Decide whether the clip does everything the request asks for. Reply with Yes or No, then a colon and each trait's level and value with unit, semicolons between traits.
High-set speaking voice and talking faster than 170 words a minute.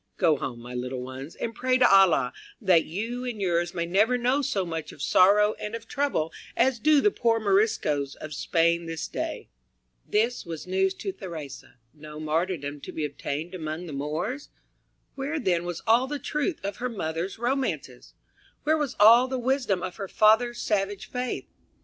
Yes: high, 195 Hz; average, 180 wpm